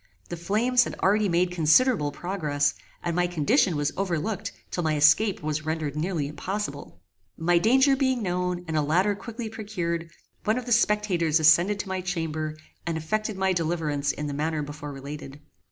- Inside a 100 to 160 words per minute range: No, average, 170 wpm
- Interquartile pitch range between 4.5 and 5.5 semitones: Yes, average, 5.0 semitones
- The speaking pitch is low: No, medium, 175 Hz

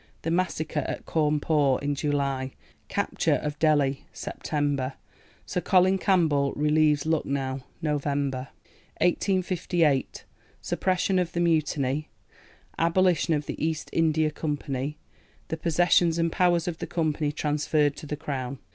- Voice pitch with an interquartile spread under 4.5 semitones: Yes, average, 2.7 semitones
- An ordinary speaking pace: No, slow, 120 wpm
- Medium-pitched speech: Yes, medium, 150 Hz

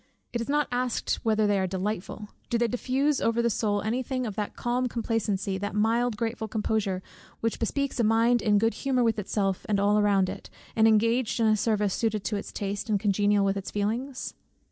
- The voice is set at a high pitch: Yes, high, 220 Hz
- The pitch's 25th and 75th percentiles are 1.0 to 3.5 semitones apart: Yes, narrow, 2.5 semitones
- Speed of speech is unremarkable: No, fast, 210 wpm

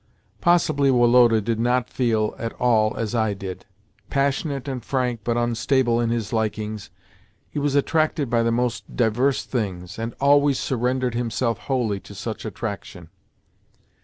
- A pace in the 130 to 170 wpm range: Yes, average, 145 wpm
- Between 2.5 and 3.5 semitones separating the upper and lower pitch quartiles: Yes, average, 3.0 semitones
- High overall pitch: No, low, 120 Hz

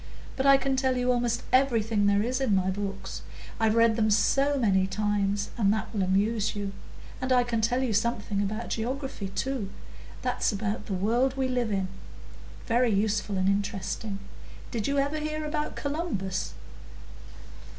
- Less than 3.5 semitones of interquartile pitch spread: No, average, 4.2 semitones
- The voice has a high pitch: Yes, high, 220 Hz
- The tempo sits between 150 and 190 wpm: Yes, average, 160 wpm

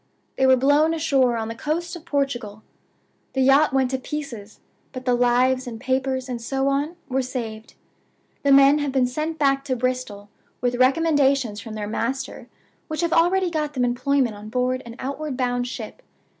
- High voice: Yes, very high, 260 Hz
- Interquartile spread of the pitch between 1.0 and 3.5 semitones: Yes, average, 2.7 semitones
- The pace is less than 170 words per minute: No, average, 180 wpm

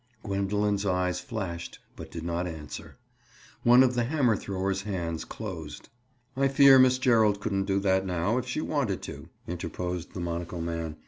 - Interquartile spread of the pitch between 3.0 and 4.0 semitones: No, average, 5.3 semitones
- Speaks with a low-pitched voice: Yes, low, 100 Hz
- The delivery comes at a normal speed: Yes, average, 170 wpm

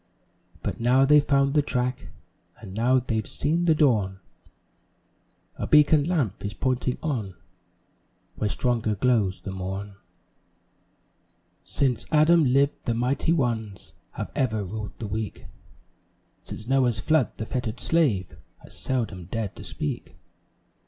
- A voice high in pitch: No, low, 120 Hz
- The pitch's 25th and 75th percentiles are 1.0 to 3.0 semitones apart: No, average, 4.8 semitones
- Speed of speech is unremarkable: No, slow, 130 wpm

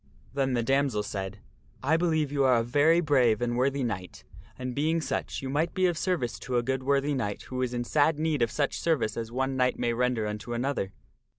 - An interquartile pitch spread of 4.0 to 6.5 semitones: No, average, 3.5 semitones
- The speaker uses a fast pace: Yes, fast, 225 wpm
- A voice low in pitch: Yes, low, 130 Hz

